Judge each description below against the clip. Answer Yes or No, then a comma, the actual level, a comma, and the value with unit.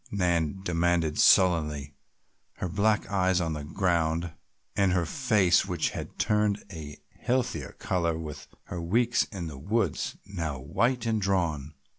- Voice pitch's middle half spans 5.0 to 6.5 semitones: No, average, 3.9 semitones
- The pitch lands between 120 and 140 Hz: No, very low, 90 Hz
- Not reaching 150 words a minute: Yes, average, 140 wpm